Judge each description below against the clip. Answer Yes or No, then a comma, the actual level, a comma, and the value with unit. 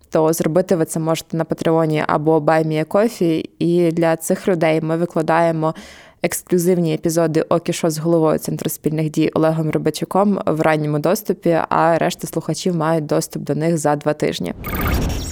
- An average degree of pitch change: No, narrow, 1.4 semitones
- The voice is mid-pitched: Yes, medium, 165 Hz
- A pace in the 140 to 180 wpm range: Yes, fast, 155 wpm